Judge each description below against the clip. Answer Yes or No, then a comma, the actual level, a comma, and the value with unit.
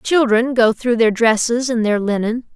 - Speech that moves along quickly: No, average, 190 wpm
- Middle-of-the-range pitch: No, high, 230 Hz